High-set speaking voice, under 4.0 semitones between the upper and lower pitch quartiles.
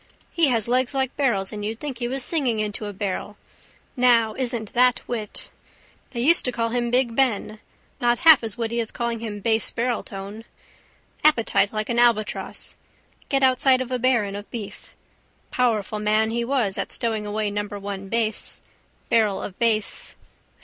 Yes: high, 230 Hz; average, 2.9 semitones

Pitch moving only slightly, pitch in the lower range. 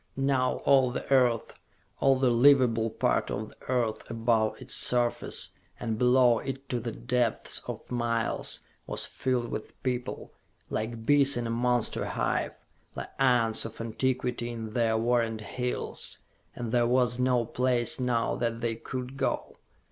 Yes: narrow, 1.8 semitones; low, 120 Hz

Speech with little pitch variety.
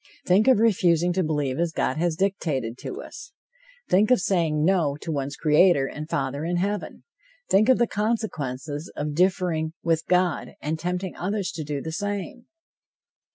No: average, 4.2 semitones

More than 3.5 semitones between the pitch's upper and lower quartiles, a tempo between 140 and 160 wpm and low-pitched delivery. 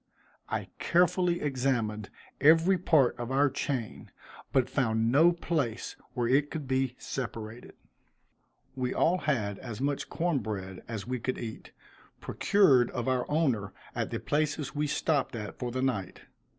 Yes: average, 4.4 semitones; average, 150 wpm; low, 130 Hz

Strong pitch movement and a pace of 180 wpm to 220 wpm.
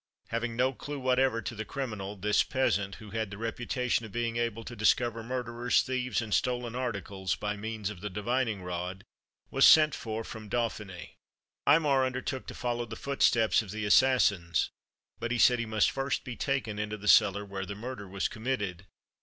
No: average, 3.4 semitones; average, 185 wpm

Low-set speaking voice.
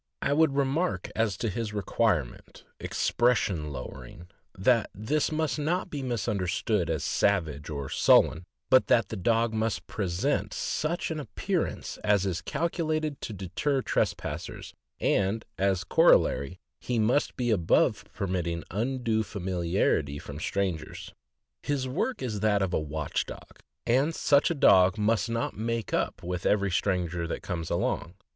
Yes: low, 105 Hz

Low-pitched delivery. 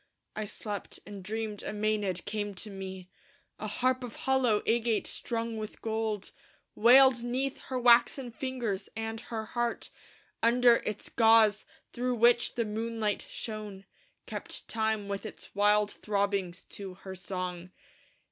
No: high, 220 Hz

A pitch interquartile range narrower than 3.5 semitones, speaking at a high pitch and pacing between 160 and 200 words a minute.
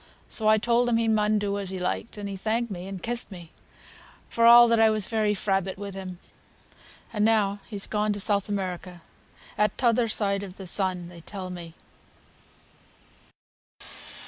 Yes: narrow, 2.6 semitones; high, 205 Hz; average, 170 wpm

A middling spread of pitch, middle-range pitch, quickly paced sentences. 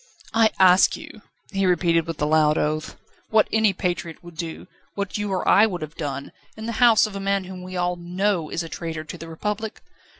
Yes: average, 3.8 semitones; medium, 180 Hz; fast, 220 wpm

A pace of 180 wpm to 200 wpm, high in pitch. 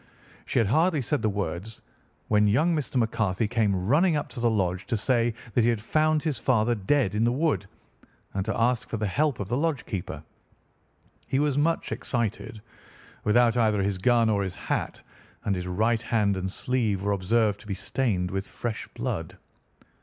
No: average, 190 wpm; low, 110 Hz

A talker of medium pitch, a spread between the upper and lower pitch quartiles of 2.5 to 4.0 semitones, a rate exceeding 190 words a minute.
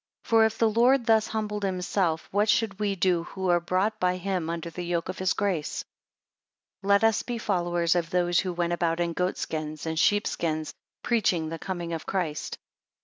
Yes: medium, 180 Hz; average, 3.4 semitones; average, 200 wpm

